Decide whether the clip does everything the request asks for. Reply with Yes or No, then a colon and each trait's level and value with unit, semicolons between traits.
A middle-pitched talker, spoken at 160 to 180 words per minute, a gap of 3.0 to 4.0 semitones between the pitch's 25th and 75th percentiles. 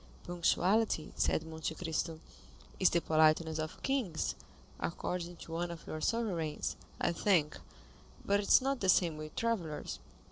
No: medium, 170 Hz; average, 145 wpm; average, 3.5 semitones